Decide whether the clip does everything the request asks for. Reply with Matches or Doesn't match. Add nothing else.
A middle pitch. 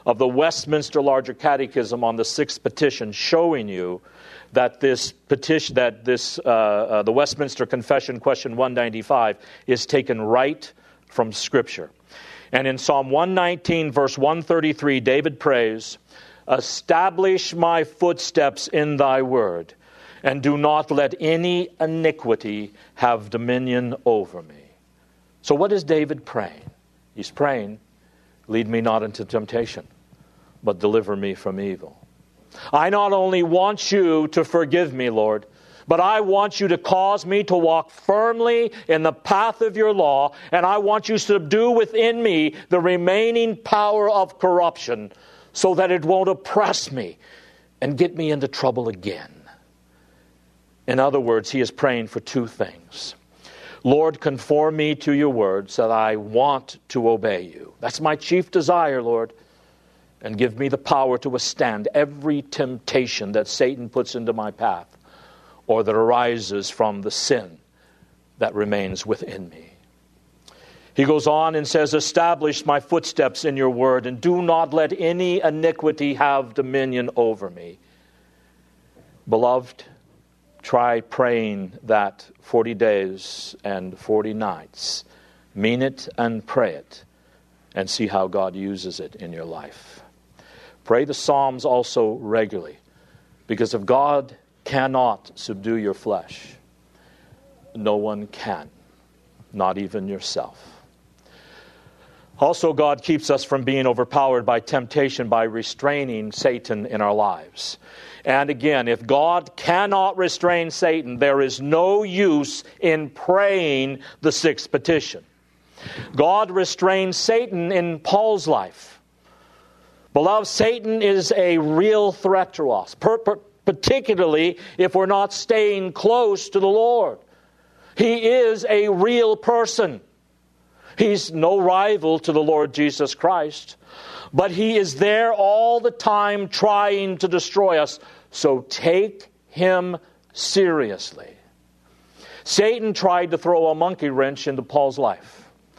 Matches